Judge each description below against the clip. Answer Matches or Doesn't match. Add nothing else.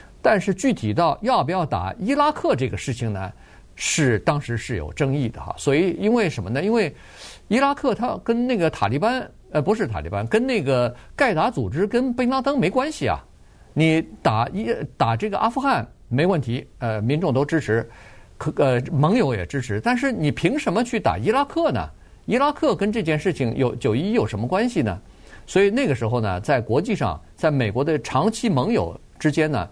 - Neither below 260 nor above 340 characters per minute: Matches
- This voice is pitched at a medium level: Matches